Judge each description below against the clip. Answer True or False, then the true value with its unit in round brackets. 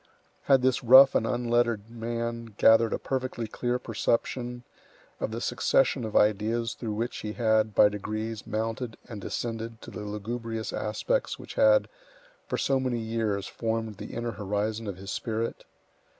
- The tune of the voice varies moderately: False (1.9 semitones)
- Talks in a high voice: False (115 Hz)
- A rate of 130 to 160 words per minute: True (155 wpm)